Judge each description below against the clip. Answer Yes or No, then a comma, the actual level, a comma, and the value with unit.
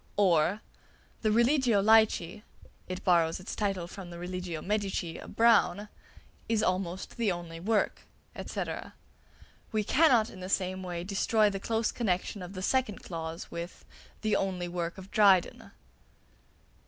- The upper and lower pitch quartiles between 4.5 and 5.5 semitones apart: No, average, 3.5 semitones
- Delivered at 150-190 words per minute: No, average, 140 wpm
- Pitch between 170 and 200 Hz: Yes, high, 190 Hz